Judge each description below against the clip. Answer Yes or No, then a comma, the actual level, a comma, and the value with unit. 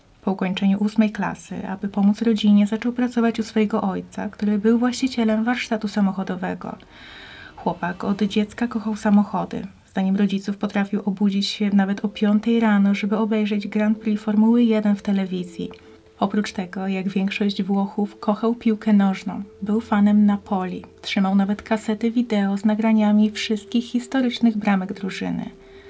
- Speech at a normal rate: Yes, average, 140 wpm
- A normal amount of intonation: No, narrow, 1.7 semitones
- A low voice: No, high, 210 Hz